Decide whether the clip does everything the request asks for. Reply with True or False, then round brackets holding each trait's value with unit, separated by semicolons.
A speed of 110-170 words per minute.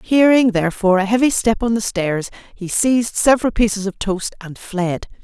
False (185 wpm)